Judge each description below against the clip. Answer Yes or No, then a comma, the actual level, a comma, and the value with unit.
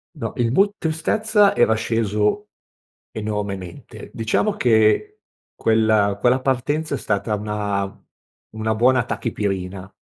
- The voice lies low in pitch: Yes, low, 110 Hz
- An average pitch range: Yes, average, 4.2 semitones